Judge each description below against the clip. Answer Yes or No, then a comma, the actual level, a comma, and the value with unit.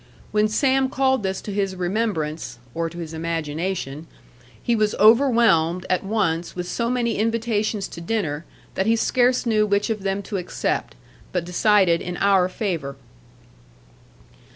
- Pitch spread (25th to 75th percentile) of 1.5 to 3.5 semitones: No, average, 4.7 semitones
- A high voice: Yes, high, 195 Hz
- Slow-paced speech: No, average, 150 wpm